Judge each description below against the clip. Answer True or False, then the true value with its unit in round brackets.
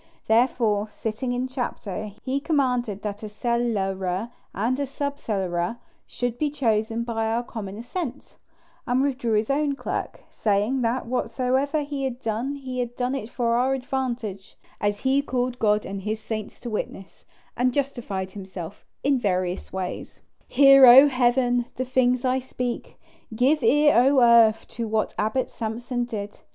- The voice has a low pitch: False (240 Hz)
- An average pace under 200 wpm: True (155 wpm)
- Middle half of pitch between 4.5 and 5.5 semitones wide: False (3.4 semitones)